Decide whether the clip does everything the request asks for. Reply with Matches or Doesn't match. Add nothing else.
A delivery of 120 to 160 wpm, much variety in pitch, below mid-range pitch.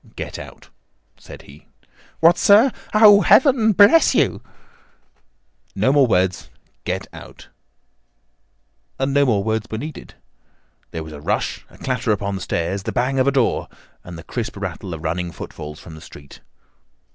Matches